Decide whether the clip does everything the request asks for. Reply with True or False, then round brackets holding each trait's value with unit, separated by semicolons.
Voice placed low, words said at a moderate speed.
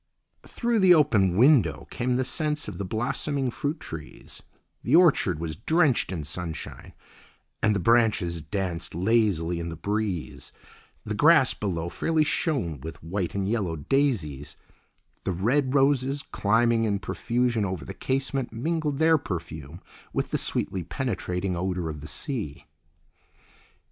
True (105 Hz; 145 wpm)